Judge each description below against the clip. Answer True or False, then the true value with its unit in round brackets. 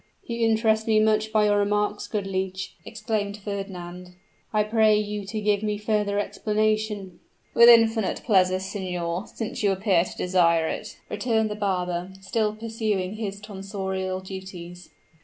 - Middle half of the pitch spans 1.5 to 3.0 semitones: True (2.4 semitones)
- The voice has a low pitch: False (205 Hz)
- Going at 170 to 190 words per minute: False (145 wpm)